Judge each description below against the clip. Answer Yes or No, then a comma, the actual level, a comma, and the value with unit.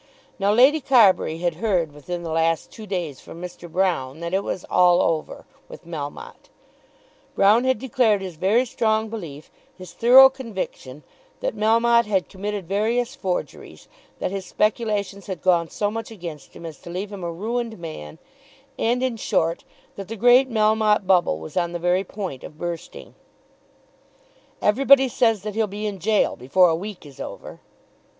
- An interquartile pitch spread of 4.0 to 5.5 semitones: Yes, average, 4.6 semitones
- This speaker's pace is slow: No, average, 170 wpm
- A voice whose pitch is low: No, high, 195 Hz